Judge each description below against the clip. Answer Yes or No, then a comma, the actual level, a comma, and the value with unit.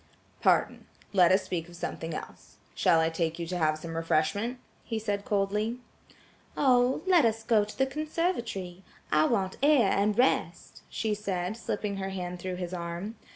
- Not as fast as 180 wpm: Yes, average, 170 wpm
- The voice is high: Yes, high, 195 Hz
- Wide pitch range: No, average, 4.6 semitones